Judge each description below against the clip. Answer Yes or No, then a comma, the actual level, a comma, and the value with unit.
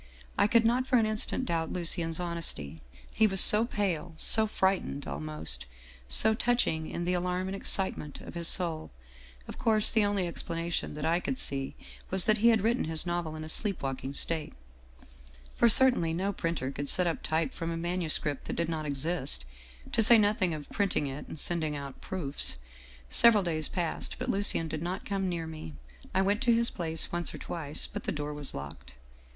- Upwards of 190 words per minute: Yes, average, 200 wpm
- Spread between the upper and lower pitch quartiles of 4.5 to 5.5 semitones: Yes, average, 5.0 semitones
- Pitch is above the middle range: No, medium, 170 Hz